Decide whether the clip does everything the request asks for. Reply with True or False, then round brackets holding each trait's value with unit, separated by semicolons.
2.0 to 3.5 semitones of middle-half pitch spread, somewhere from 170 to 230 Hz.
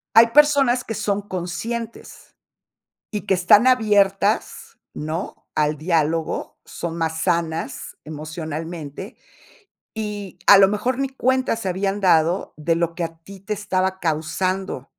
False (4.3 semitones; 190 Hz)